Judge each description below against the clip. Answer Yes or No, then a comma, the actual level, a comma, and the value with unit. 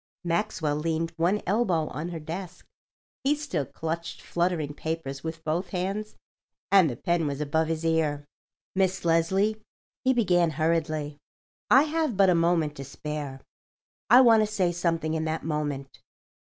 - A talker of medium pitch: Yes, medium, 165 Hz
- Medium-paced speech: Yes, average, 150 wpm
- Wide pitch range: No, average, 3.4 semitones